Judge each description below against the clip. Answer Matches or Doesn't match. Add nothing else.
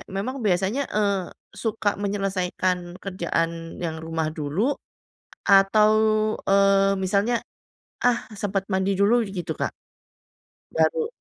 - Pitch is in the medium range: Doesn't match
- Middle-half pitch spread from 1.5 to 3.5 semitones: Matches